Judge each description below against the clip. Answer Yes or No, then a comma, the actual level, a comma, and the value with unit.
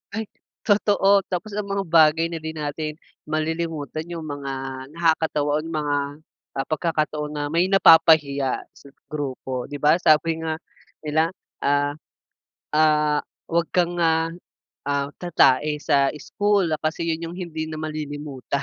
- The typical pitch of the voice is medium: Yes, medium, 155 Hz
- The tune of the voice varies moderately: No, narrow, 2.1 semitones